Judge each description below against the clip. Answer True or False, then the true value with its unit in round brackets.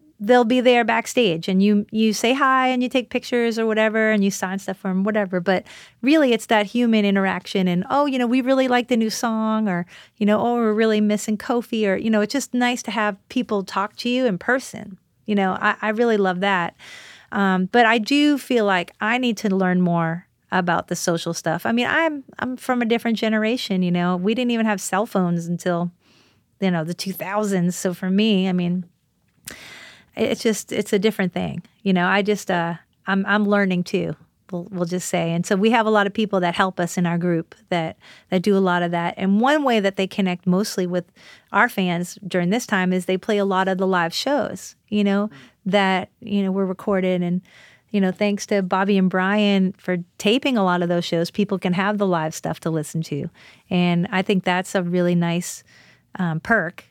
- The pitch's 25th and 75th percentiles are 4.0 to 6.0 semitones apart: False (3.6 semitones)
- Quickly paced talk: True (220 wpm)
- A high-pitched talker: True (200 Hz)